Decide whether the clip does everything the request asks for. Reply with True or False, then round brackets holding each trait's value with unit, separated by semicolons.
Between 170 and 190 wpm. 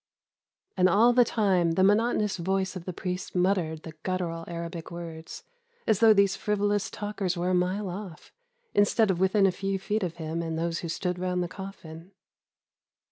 True (180 wpm)